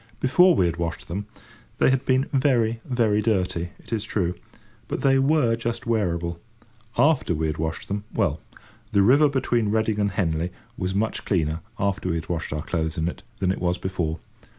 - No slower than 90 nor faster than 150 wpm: No, average, 185 wpm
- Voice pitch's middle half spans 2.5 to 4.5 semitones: No, wide, 5.5 semitones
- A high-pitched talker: No, low, 100 Hz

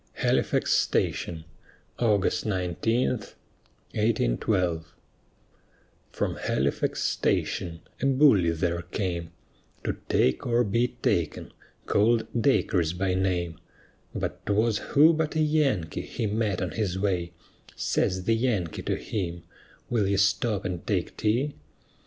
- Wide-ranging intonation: No, average, 5.0 semitones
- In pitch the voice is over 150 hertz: No, low, 100 Hz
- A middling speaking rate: No, slow, 115 wpm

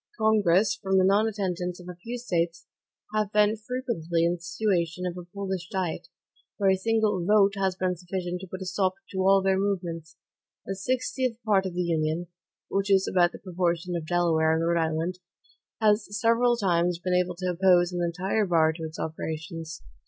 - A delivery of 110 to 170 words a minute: No, average, 185 wpm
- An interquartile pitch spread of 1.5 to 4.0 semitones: Yes, average, 2.7 semitones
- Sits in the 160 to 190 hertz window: Yes, medium, 185 Hz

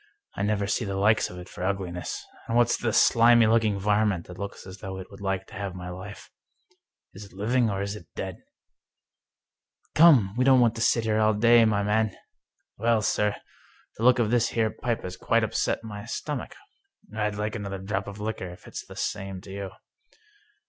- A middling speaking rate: No, fast, 210 wpm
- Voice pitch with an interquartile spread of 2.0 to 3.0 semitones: Yes, average, 2.7 semitones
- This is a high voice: No, low, 105 Hz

